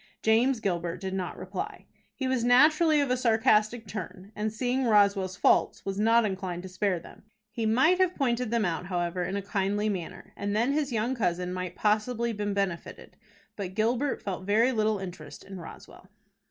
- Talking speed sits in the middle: Yes, average, 180 wpm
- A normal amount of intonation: Yes, average, 4.1 semitones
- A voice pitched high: Yes, high, 210 Hz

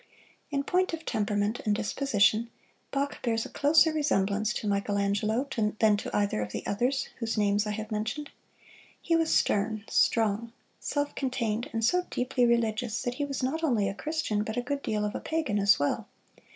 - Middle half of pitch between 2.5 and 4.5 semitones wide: No, average, 5.1 semitones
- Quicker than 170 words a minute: Yes, average, 180 wpm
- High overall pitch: Yes, high, 225 Hz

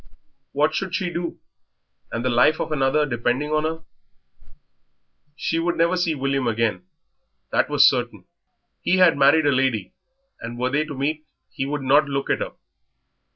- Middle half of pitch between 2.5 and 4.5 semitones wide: Yes, average, 3.3 semitones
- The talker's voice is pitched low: No, medium, 145 Hz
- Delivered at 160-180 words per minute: Yes, average, 165 wpm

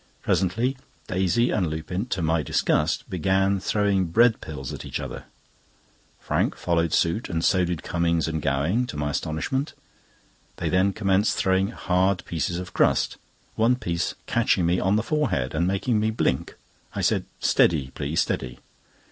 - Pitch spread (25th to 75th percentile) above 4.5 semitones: No, average, 3.8 semitones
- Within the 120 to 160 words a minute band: Yes, average, 155 wpm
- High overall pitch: No, very low, 90 Hz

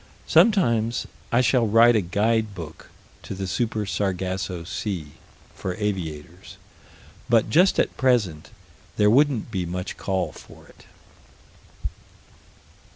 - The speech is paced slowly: Yes, slow, 115 wpm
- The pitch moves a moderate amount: Yes, average, 4.2 semitones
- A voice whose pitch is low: Yes, low, 105 Hz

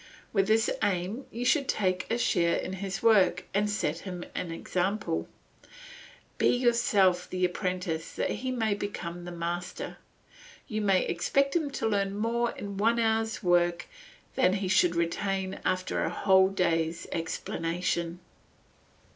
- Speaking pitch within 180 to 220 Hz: Yes, high, 190 Hz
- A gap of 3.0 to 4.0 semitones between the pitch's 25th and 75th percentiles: Yes, average, 3.6 semitones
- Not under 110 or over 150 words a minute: Yes, average, 145 wpm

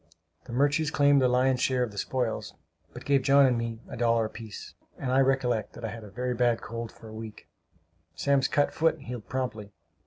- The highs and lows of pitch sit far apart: No, average, 2.9 semitones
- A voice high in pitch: No, low, 125 Hz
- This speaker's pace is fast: Yes, fast, 210 wpm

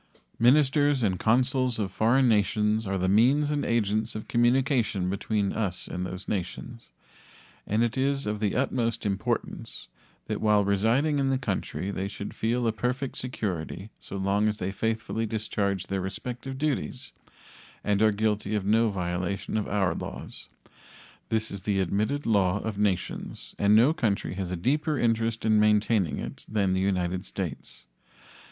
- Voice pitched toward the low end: Yes, low, 105 Hz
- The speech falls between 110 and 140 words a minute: No, average, 160 wpm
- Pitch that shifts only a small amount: No, average, 3.5 semitones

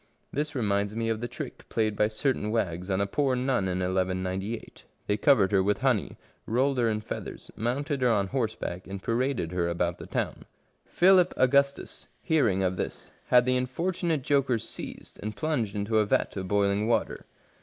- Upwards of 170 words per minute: Yes, average, 180 wpm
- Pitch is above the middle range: No, low, 110 Hz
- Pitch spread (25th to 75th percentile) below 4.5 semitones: No, average, 4.9 semitones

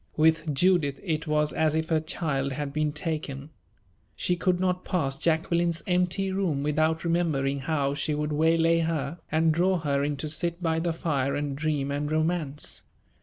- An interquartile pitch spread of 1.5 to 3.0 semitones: Yes, narrow, 2.6 semitones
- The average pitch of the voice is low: No, medium, 155 Hz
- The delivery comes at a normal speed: Yes, average, 170 wpm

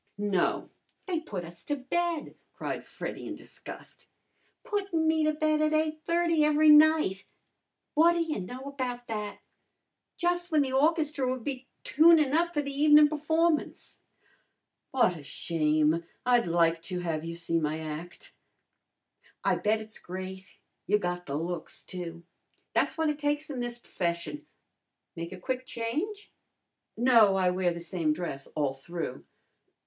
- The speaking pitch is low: No, high, 245 Hz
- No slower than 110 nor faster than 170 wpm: Yes, average, 150 wpm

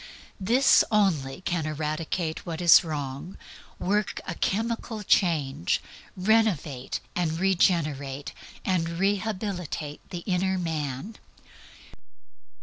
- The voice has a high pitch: No, medium, 175 Hz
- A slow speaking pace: Yes, slow, 90 wpm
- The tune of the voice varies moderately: Yes, average, 4.2 semitones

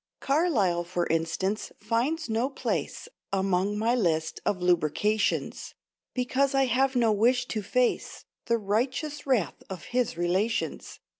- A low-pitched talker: No, high, 220 Hz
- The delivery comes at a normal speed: No, slow, 130 wpm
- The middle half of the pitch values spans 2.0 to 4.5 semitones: No, wide, 5.4 semitones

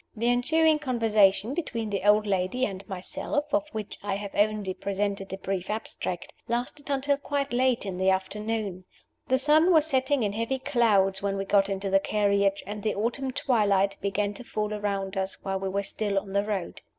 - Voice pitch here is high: Yes, high, 210 Hz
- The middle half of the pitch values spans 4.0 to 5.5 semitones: Yes, average, 4.3 semitones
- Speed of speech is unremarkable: Yes, average, 190 wpm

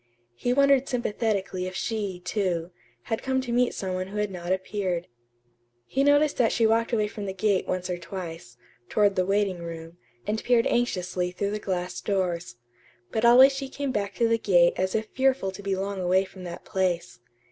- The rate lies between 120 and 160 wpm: No, average, 195 wpm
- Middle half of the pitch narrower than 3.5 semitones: No, average, 4.0 semitones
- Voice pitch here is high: Yes, high, 195 Hz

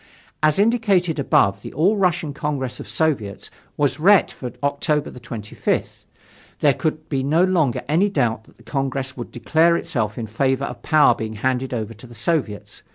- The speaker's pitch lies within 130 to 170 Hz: Yes, medium, 140 Hz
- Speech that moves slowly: No, average, 170 wpm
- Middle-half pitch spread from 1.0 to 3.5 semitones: No, average, 4.9 semitones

